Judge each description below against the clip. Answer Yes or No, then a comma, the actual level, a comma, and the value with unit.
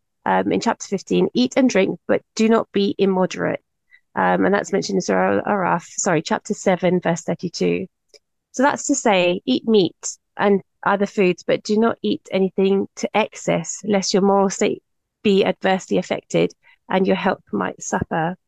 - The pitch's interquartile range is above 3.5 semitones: No, average, 3.1 semitones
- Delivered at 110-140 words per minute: No, average, 170 wpm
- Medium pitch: No, high, 195 Hz